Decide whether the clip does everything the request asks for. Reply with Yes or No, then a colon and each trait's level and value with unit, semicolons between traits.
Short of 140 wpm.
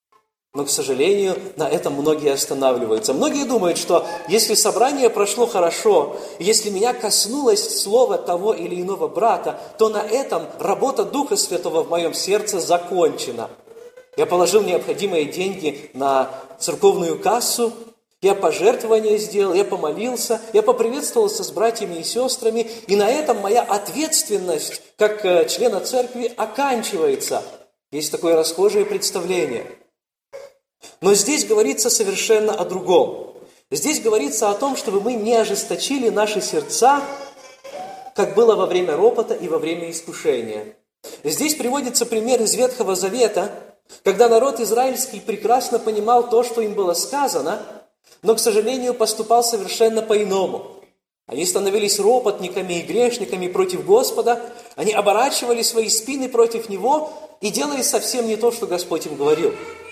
Yes: average, 130 wpm